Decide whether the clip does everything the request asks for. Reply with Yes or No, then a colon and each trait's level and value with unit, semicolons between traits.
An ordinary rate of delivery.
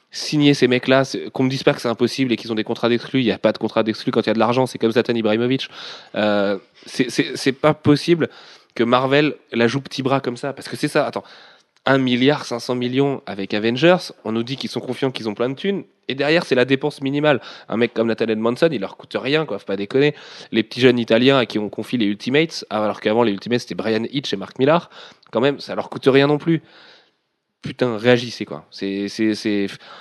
No: fast, 245 wpm